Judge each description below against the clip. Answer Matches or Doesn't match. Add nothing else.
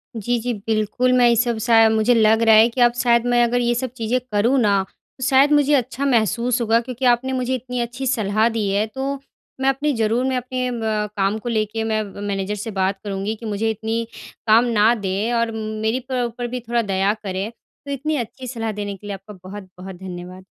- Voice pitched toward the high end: Matches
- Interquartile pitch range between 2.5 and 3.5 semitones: Matches